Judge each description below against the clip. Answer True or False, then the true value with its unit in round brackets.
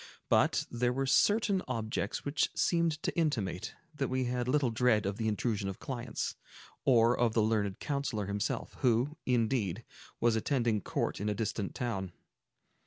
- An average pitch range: True (3.6 semitones)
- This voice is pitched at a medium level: False (120 Hz)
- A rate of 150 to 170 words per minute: True (160 wpm)